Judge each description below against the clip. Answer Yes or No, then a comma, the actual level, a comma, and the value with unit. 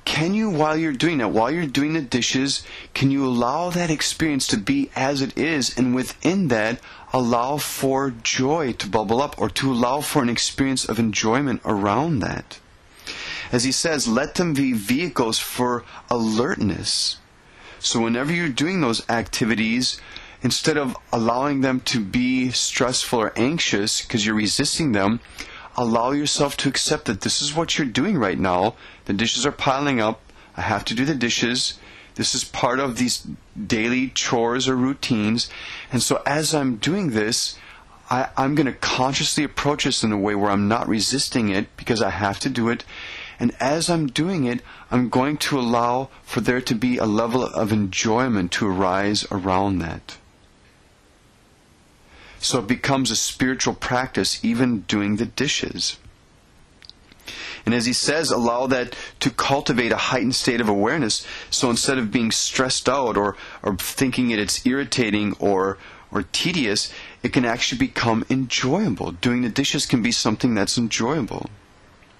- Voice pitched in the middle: No, low, 125 Hz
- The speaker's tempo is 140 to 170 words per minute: Yes, average, 165 wpm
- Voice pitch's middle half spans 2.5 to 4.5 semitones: Yes, average, 3.7 semitones